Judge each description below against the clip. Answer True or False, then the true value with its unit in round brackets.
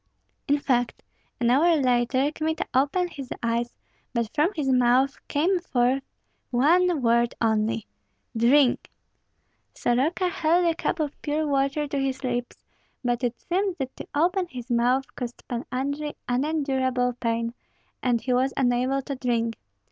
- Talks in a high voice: True (265 Hz)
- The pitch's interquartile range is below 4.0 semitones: True (3.6 semitones)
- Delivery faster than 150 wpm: False (145 wpm)